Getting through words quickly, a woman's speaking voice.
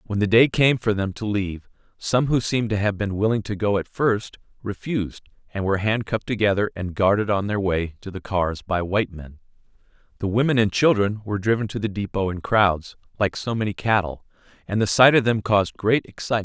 No: fast, 225 wpm; male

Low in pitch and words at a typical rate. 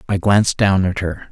No: very low, 95 Hz; fast, 230 wpm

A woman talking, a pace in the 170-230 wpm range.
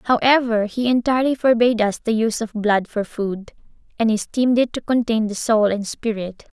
Yes: female; average, 180 wpm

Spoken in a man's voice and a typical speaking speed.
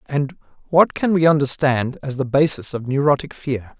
Yes: male; average, 175 wpm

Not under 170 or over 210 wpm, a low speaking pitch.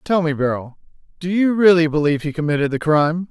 No: average, 200 wpm; medium, 160 Hz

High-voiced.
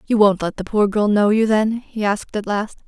Yes: high, 210 Hz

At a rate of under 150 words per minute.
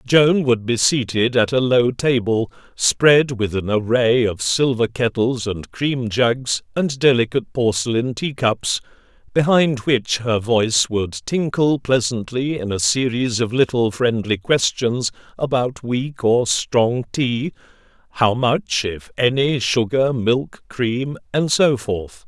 Yes: average, 140 wpm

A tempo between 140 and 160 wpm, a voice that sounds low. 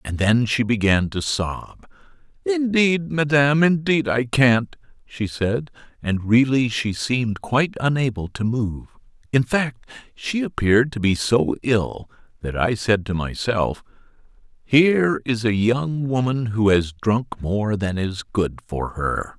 Yes: average, 150 wpm; low, 120 Hz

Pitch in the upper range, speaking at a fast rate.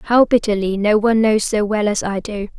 Yes: high, 210 Hz; fast, 230 wpm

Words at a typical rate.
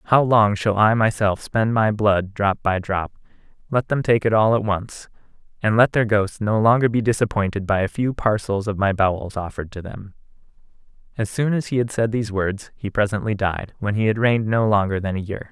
No: fast, 215 wpm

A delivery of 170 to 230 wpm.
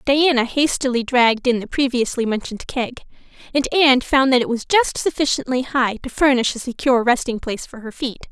Yes: average, 190 wpm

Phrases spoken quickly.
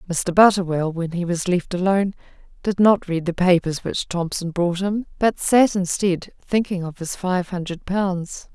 No: average, 175 wpm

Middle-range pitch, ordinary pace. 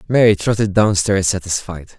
No: low, 100 Hz; average, 150 wpm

